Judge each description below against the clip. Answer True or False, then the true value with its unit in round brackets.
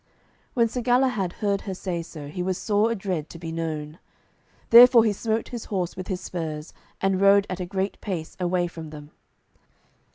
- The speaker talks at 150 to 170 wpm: False (185 wpm)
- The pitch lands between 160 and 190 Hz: True (185 Hz)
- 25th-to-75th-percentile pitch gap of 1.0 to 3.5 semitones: False (4.1 semitones)